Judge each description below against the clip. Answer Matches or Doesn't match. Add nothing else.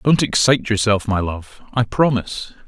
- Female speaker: Doesn't match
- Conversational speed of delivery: Matches